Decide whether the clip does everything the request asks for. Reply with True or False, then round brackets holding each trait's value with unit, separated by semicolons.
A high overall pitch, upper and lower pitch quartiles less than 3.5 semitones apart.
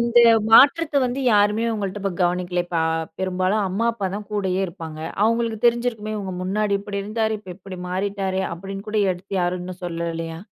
True (195 Hz; 3.0 semitones)